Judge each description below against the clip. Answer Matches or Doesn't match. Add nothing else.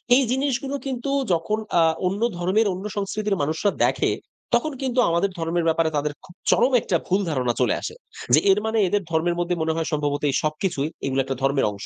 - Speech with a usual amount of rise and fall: Doesn't match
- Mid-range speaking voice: Matches